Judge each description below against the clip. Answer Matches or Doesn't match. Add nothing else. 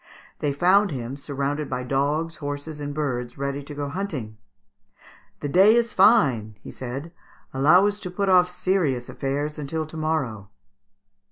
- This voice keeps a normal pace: Matches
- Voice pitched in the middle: Matches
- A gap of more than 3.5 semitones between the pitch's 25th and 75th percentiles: Matches